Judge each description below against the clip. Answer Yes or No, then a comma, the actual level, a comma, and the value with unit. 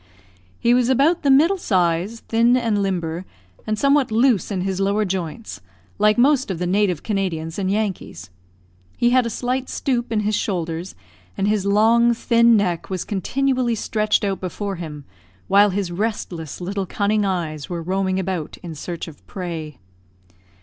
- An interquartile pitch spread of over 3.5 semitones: Yes, average, 4.6 semitones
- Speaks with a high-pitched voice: Yes, high, 200 Hz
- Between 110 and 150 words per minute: No, average, 165 wpm